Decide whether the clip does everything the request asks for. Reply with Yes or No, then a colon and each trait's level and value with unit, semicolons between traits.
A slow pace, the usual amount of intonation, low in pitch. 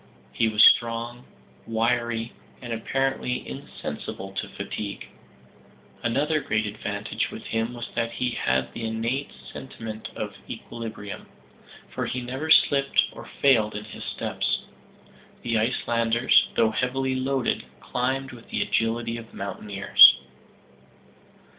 No: slow, 120 wpm; narrow, 2.2 semitones; low, 115 Hz